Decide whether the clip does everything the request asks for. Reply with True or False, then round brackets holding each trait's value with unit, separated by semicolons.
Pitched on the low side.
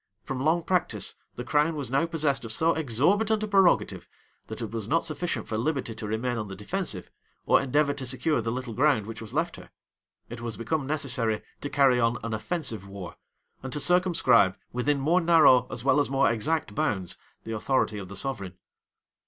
True (130 Hz)